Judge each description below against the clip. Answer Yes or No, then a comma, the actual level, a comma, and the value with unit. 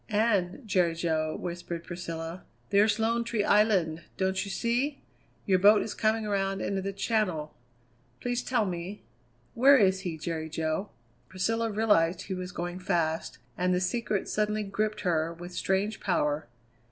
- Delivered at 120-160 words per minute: Yes, average, 155 wpm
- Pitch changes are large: No, average, 3.8 semitones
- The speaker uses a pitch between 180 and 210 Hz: Yes, high, 190 Hz